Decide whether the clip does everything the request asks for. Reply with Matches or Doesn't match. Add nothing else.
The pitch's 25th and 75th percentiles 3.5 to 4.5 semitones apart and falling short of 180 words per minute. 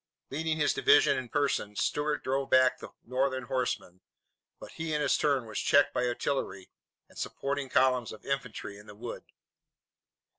Doesn't match